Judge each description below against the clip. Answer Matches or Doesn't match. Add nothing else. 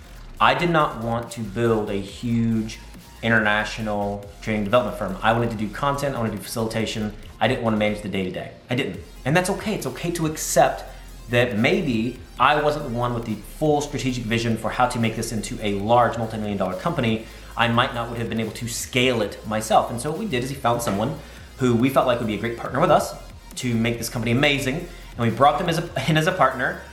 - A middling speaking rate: Doesn't match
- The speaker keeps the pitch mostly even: Doesn't match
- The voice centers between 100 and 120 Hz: Matches